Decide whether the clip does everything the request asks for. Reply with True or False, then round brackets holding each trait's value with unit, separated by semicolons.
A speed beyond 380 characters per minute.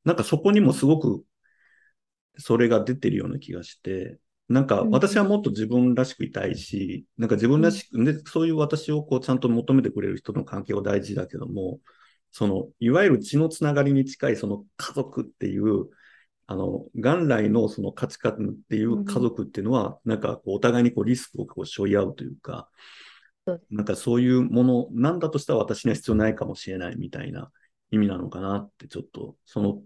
True (390 characters per minute)